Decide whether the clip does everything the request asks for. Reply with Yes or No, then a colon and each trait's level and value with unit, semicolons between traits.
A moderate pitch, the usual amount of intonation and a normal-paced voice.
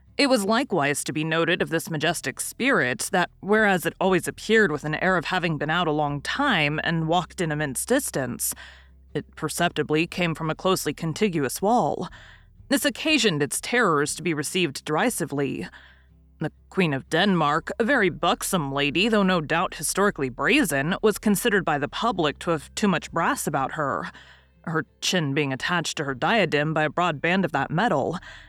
Yes: medium, 165 Hz; average, 4.3 semitones; average, 180 wpm